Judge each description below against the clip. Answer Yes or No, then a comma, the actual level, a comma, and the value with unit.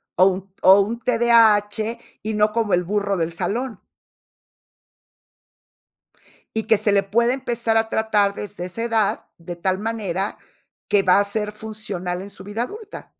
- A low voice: No, high, 210 Hz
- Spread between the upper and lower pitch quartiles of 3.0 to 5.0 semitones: No, narrow, 2.6 semitones